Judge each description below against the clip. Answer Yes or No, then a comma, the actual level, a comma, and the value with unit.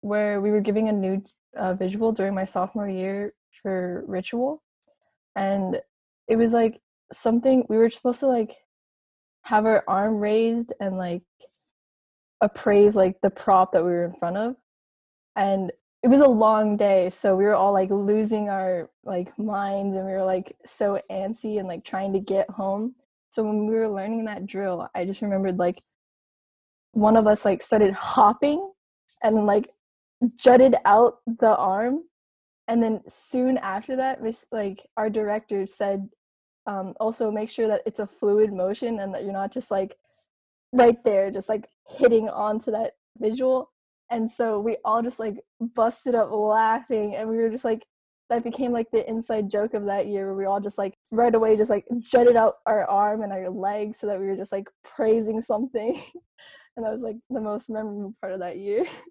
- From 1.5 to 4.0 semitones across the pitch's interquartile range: Yes, average, 2.9 semitones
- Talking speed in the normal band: Yes, average, 185 wpm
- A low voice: No, high, 215 Hz